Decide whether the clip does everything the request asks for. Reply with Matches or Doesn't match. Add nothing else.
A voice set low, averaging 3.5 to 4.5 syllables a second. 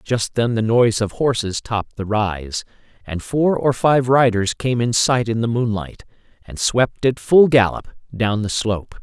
Matches